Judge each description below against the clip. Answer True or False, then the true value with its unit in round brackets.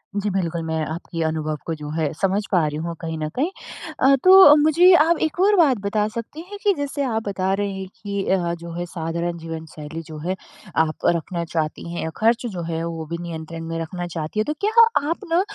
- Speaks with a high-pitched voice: False (175 Hz)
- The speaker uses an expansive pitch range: True (7.5 semitones)